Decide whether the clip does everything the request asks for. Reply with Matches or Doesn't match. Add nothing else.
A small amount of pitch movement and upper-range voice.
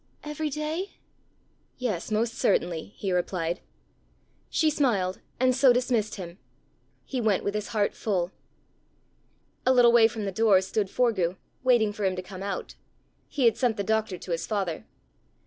Doesn't match